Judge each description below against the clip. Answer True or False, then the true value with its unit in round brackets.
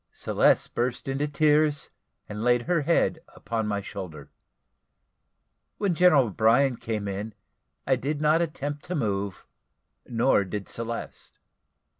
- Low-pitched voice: True (120 Hz)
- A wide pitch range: True (5.9 semitones)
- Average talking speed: False (125 wpm)